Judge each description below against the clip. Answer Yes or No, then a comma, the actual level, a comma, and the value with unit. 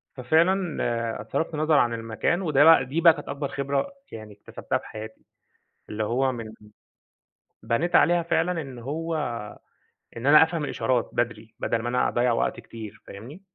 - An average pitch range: No, wide, 5.9 semitones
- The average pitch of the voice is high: No, low, 135 Hz